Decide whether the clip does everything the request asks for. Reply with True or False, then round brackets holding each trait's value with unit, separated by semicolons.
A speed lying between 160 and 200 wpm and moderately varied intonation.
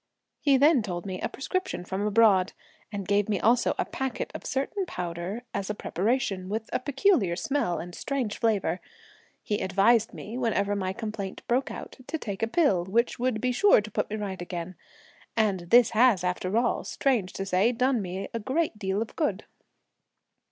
True (185 wpm; 4.7 semitones)